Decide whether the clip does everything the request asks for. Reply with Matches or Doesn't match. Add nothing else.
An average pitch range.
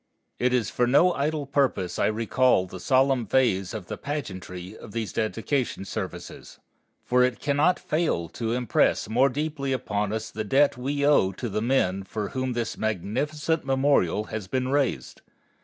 Matches